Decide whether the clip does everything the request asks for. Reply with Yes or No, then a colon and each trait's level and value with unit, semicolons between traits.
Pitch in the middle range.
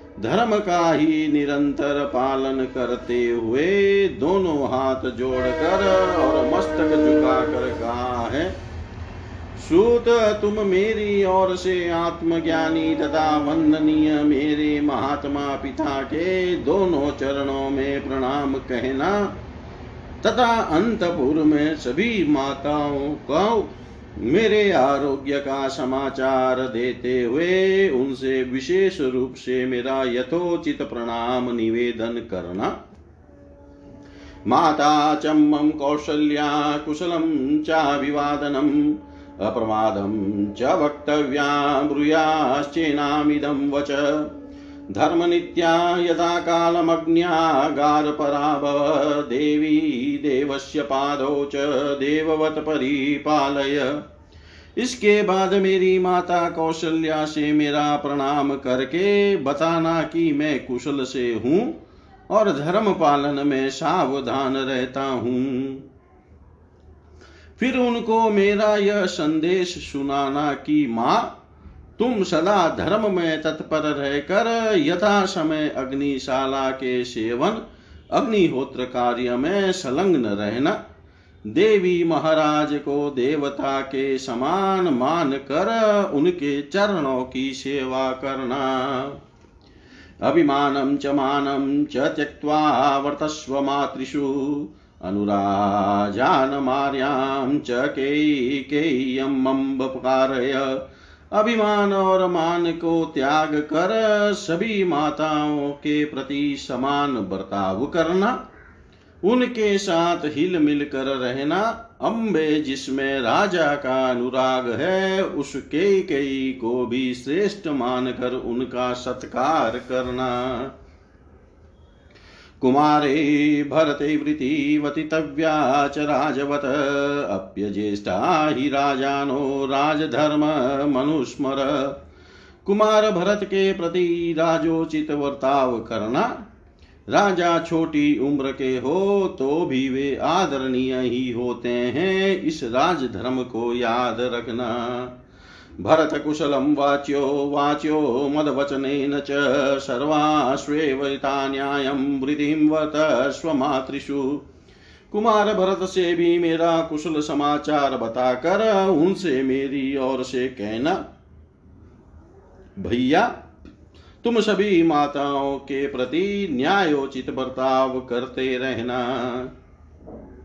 Yes: medium, 145 Hz